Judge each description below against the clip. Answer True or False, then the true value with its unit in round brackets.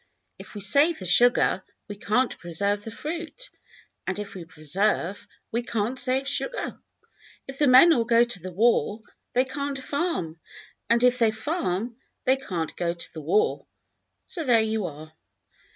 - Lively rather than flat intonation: True (5.9 semitones)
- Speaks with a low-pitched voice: False (230 Hz)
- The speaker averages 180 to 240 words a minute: False (165 wpm)